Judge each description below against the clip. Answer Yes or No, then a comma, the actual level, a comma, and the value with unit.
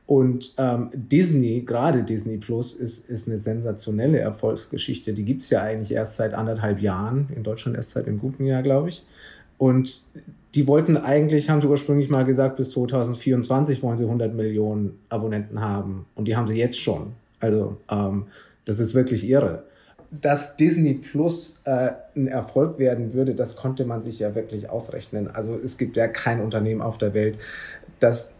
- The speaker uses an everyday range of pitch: Yes, average, 3.4 semitones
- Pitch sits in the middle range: No, low, 120 Hz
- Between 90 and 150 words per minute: No, average, 175 wpm